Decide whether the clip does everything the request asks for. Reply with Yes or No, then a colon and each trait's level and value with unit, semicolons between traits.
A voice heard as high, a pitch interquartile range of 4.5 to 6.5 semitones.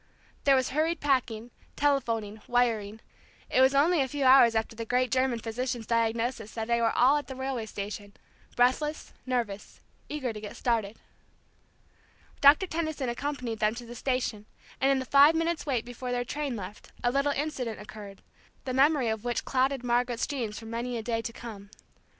No: high, 245 Hz; average, 3.3 semitones